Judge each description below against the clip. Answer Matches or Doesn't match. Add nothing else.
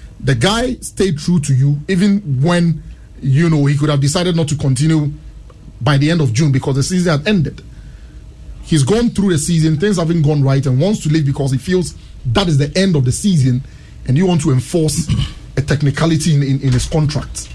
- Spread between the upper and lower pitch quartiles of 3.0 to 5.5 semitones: Matches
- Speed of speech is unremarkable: Doesn't match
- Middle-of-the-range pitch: Matches